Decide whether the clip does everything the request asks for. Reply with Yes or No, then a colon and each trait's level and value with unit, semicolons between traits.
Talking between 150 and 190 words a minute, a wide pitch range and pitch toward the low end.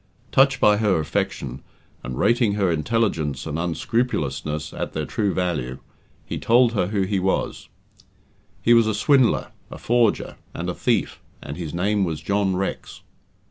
Yes: average, 155 wpm; wide, 6.3 semitones; very low, 95 Hz